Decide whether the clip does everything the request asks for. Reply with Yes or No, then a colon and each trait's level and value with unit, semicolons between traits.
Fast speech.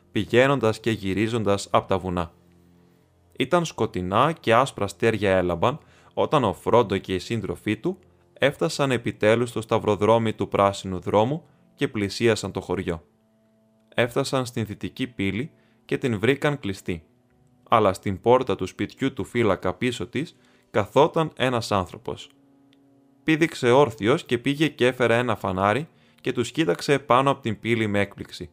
No: average, 140 wpm